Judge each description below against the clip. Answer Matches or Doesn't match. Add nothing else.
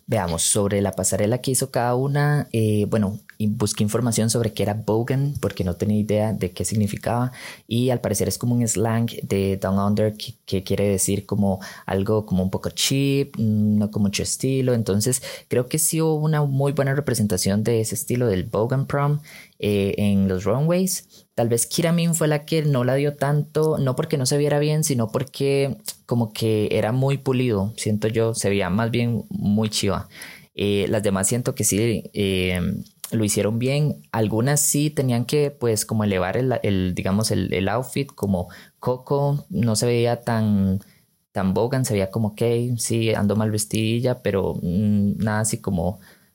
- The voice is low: Matches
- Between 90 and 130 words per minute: Doesn't match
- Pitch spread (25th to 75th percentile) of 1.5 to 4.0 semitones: Doesn't match